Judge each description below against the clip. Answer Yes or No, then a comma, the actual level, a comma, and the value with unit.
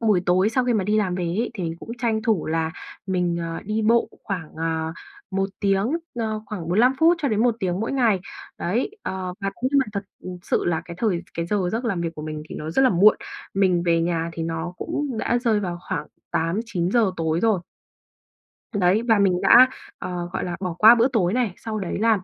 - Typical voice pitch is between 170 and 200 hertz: Yes, high, 195 Hz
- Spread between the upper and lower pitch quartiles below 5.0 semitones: Yes, average, 4.6 semitones